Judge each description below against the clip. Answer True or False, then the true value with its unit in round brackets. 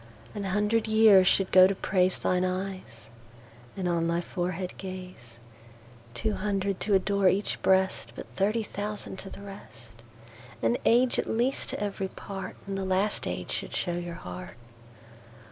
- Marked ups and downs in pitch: True (7.6 semitones)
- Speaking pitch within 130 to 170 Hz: False (185 Hz)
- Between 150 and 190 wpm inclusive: False (140 wpm)